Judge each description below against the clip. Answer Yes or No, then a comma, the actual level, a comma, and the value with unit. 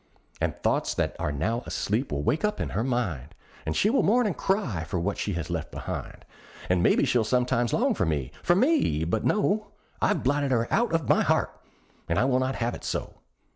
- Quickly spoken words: Yes, fast, 215 wpm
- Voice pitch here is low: Yes, low, 120 Hz